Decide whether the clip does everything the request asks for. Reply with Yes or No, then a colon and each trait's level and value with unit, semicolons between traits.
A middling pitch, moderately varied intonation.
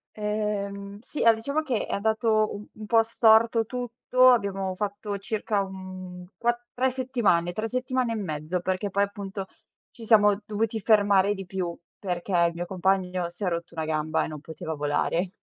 No: high, 200 Hz; average, 3.5 semitones